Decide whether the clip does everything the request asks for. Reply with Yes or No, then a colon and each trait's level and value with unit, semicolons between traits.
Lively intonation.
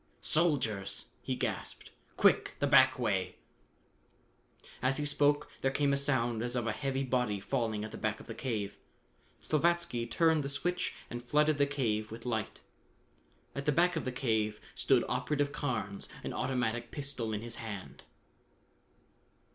No: average, 4.4 semitones